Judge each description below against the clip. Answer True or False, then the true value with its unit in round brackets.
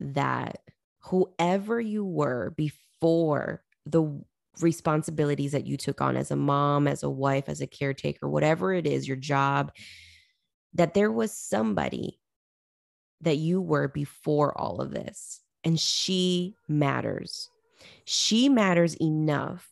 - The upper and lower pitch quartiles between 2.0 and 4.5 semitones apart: True (4.2 semitones)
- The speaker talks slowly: True (130 wpm)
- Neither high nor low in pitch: True (155 Hz)